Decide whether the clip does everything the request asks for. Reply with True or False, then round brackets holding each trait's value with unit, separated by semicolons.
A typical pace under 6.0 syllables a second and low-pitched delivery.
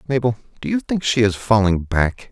True (5.2 syllables/s; 115 Hz)